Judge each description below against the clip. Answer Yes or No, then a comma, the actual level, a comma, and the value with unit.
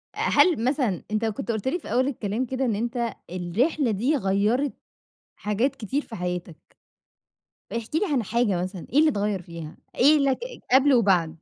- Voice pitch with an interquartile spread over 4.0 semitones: Yes, average, 5.3 semitones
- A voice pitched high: Yes, high, 230 Hz